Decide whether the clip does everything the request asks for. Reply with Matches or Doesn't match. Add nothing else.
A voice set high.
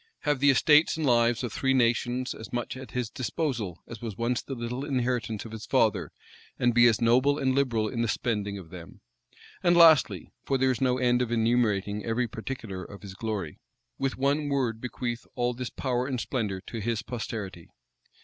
Doesn't match